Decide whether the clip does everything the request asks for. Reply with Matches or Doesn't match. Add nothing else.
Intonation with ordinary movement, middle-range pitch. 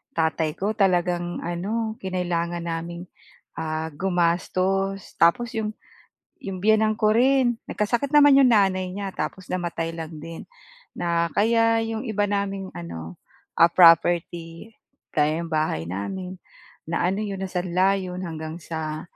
Matches